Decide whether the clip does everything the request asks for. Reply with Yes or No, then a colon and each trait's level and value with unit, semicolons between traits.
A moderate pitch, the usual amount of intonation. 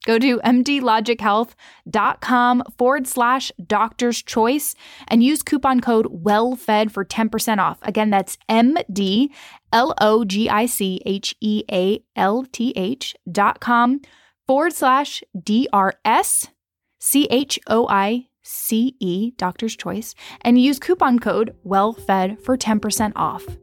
No: high, 225 Hz; average, 3.5 semitones